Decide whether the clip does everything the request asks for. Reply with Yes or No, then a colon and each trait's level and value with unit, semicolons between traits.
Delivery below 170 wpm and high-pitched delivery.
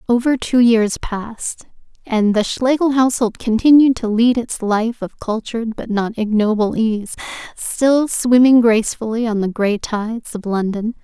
Yes: average, 150 wpm; high, 230 Hz